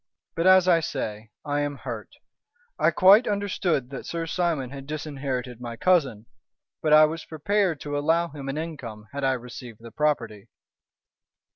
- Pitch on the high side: No, medium, 145 Hz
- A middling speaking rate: Yes, average, 160 wpm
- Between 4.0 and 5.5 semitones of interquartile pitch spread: Yes, average, 4.7 semitones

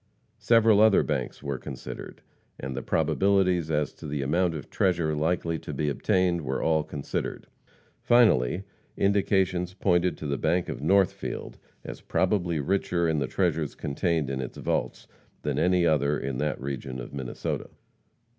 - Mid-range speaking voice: No, very low, 80 Hz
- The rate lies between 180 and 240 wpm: No, average, 155 wpm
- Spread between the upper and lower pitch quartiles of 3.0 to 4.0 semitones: No, average, 4.5 semitones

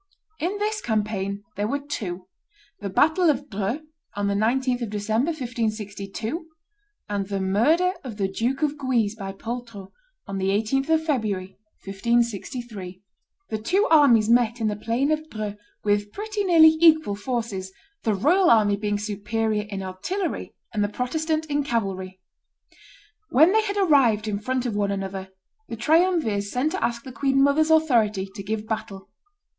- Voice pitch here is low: No, high, 225 Hz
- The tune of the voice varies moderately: No, wide, 6.1 semitones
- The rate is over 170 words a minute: No, average, 160 wpm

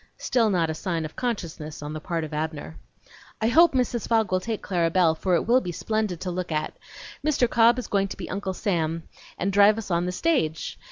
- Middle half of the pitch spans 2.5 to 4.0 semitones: No, wide, 5.4 semitones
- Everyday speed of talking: No, fast, 225 wpm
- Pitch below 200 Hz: Yes, medium, 185 Hz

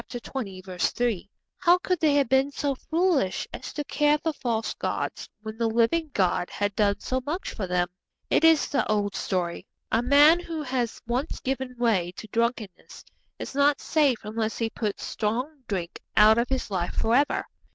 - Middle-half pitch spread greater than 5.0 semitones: Yes, wide, 5.4 semitones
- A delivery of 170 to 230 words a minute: Yes, average, 175 wpm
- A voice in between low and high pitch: No, high, 240 Hz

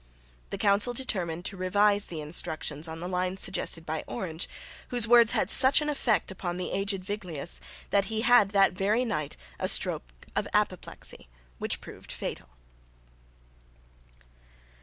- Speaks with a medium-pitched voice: No, high, 195 Hz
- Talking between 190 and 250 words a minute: No, average, 145 wpm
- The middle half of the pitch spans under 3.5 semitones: No, average, 4.3 semitones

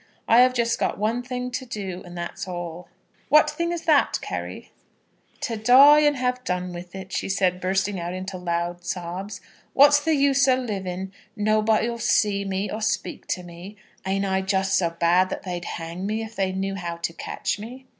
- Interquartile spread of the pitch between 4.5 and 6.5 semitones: Yes, average, 4.9 semitones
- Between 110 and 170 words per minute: No, average, 195 wpm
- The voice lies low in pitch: No, high, 195 Hz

